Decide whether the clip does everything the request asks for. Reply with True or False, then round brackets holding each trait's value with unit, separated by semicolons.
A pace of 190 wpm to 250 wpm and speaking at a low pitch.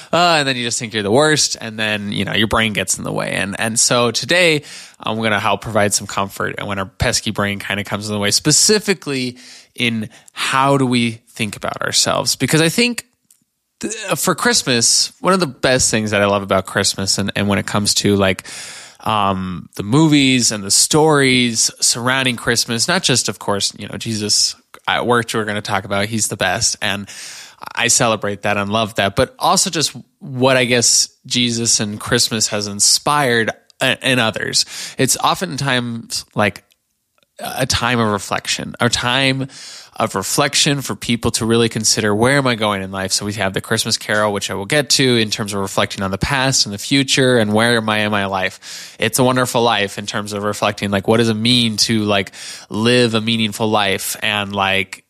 True (205 wpm; 115 Hz)